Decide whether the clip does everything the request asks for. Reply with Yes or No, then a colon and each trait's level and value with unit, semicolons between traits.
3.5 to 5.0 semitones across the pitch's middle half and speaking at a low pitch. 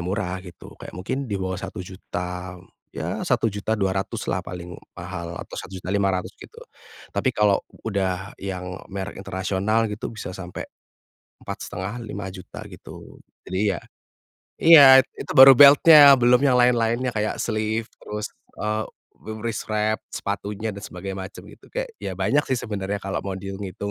No: average, 3.1 semitones; low, 100 Hz